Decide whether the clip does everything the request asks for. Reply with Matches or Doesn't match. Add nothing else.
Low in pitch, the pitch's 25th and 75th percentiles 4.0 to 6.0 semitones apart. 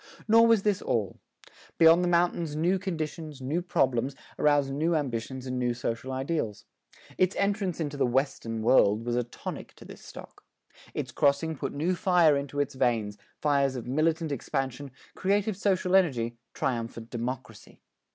Doesn't match